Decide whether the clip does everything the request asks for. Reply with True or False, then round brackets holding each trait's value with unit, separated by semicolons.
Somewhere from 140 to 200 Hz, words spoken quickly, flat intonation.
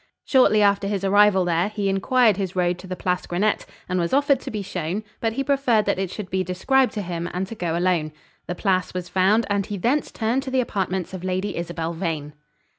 False (190 Hz; 225 wpm; 3.1 semitones)